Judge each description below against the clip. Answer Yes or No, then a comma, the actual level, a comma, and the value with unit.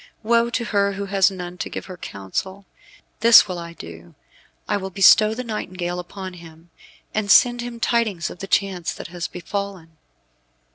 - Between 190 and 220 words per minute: No, average, 175 wpm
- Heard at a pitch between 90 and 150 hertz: No, high, 190 Hz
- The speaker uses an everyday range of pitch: Yes, average, 3.3 semitones